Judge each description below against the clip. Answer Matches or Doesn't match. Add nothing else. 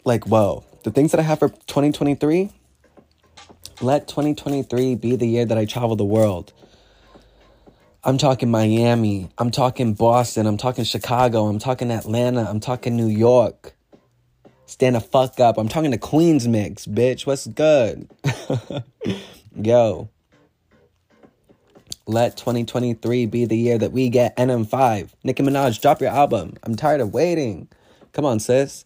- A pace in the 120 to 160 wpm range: Matches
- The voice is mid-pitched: Doesn't match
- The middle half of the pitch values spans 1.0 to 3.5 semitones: Matches